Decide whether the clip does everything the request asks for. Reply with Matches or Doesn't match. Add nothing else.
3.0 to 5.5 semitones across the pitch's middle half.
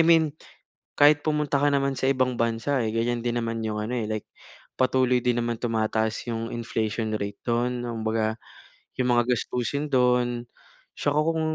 Doesn't match